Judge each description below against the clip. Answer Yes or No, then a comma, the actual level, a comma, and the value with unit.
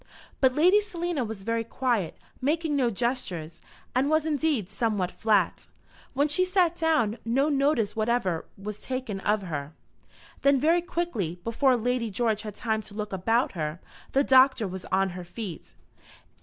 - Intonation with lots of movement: Yes, wide, 6.0 semitones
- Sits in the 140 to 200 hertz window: No, high, 230 Hz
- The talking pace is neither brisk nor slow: Yes, average, 155 wpm